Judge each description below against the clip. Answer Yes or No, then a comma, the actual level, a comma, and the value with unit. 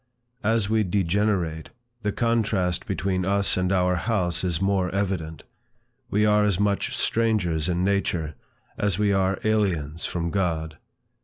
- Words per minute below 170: Yes, average, 140 wpm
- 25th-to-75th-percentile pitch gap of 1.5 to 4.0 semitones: Yes, average, 2.9 semitones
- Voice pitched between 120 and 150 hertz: No, very low, 95 Hz